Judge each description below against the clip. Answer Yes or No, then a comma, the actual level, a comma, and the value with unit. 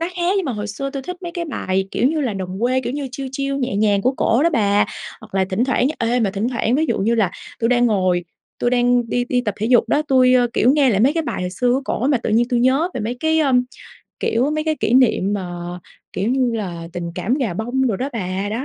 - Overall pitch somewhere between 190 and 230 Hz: No, high, 245 Hz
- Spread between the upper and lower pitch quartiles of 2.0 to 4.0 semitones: No, average, 4.5 semitones